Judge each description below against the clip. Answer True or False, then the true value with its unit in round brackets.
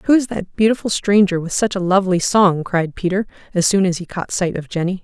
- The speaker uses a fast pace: True (240 wpm)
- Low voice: False (190 Hz)